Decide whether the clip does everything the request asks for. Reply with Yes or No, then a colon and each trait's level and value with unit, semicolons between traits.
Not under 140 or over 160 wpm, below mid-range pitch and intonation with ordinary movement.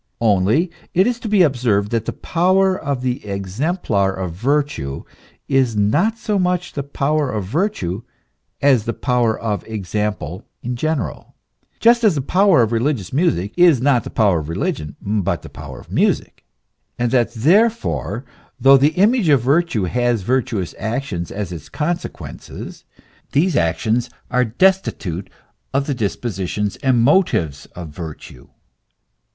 No: average, 150 wpm; low, 125 Hz; wide, 7.8 semitones